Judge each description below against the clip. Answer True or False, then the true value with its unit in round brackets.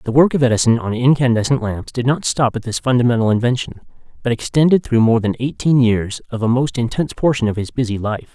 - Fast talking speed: True (215 wpm)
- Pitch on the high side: False (120 Hz)